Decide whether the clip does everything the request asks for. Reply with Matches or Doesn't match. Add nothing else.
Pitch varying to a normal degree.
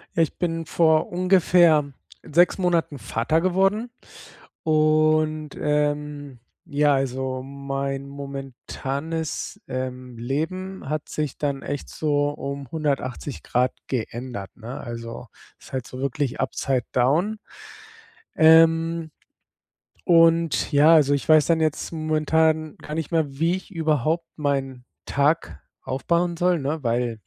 Matches